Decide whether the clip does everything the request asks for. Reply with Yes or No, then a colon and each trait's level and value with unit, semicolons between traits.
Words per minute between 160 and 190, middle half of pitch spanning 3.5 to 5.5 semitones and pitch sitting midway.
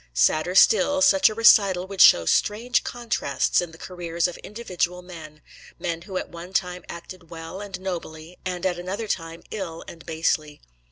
No: average, 170 wpm; average, 2.9 semitones; medium, 180 Hz